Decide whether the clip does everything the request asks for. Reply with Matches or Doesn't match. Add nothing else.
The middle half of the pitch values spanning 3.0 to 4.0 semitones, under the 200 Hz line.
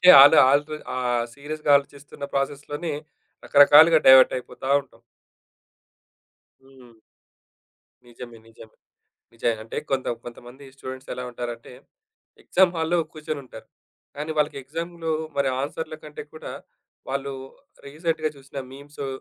Matches